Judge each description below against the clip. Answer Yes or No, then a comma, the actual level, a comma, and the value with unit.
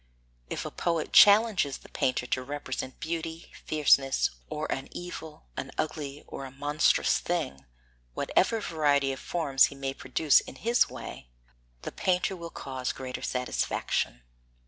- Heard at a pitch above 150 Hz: No, medium, 145 Hz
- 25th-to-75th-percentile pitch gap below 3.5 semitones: No, average, 3.8 semitones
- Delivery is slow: No, average, 145 wpm